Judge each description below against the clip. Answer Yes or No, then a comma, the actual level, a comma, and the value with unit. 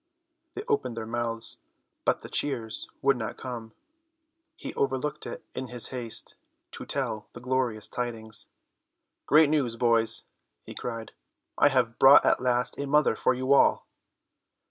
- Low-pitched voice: Yes, low, 125 Hz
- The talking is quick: No, average, 145 wpm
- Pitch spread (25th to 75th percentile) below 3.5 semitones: Yes, average, 2.7 semitones